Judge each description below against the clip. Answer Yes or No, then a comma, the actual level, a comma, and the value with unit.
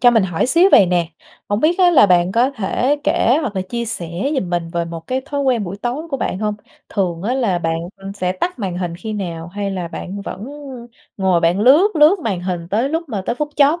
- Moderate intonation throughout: No, wide, 6.7 semitones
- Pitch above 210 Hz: No, high, 205 Hz